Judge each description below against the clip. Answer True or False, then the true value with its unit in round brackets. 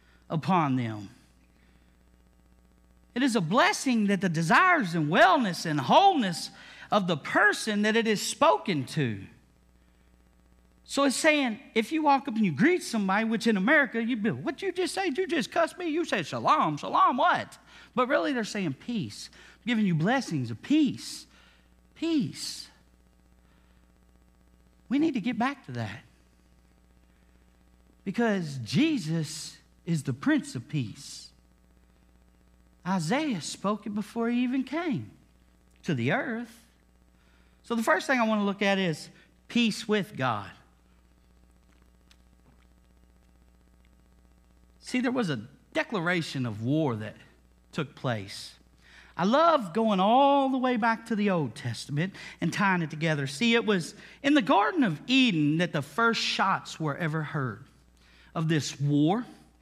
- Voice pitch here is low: False (160 Hz)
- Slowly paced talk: False (145 wpm)